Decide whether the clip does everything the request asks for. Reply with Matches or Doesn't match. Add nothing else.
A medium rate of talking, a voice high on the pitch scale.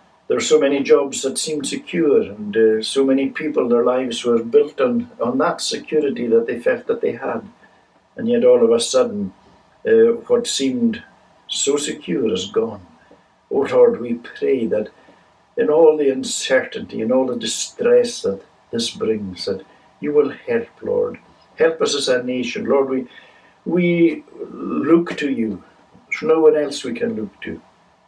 Matches